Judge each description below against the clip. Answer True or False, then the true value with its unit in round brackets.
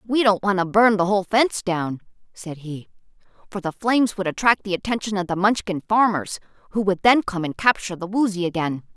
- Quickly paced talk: True (210 wpm)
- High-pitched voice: True (195 Hz)